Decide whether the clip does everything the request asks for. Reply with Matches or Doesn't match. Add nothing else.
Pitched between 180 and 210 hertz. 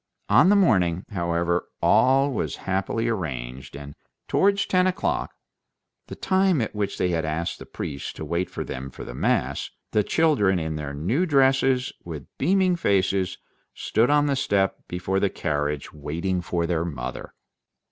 Doesn't match